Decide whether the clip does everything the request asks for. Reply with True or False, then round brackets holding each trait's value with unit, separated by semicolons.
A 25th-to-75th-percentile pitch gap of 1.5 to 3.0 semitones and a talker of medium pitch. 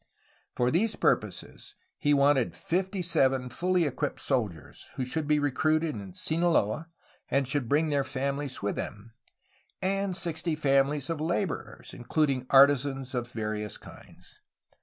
False (4.0 semitones; 145 Hz)